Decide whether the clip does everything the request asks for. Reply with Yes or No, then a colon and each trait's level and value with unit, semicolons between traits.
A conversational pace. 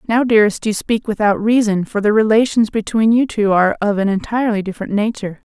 Yes: average, 195 wpm